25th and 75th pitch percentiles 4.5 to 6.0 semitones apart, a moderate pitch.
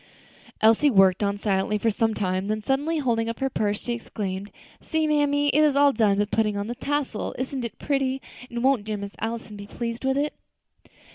No: average, 4.8 semitones; high, 230 Hz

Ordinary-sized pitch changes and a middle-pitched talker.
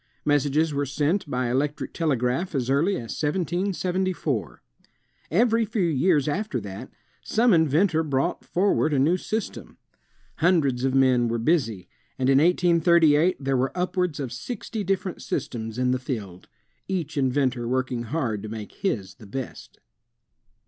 No: wide, 5.7 semitones; medium, 145 Hz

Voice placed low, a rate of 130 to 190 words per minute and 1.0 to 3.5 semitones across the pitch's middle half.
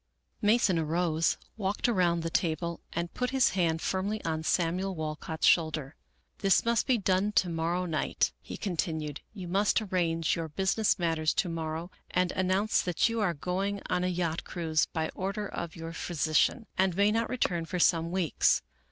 No: medium, 175 Hz; average, 180 wpm; average, 3.1 semitones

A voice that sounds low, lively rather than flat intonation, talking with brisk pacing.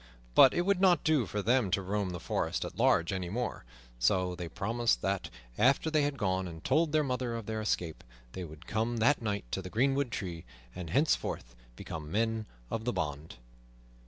No: low, 110 Hz; wide, 6.1 semitones; average, 195 wpm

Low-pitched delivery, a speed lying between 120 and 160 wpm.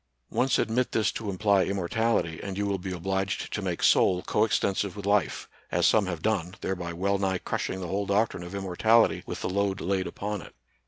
No: low, 100 Hz; fast, 205 wpm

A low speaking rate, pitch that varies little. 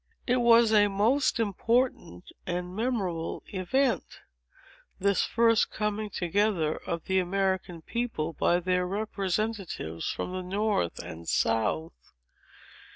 No: slow, 105 wpm; average, 4.1 semitones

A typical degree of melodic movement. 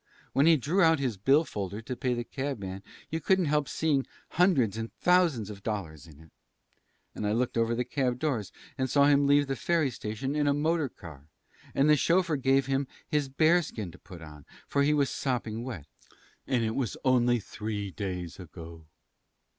No: wide, 5.8 semitones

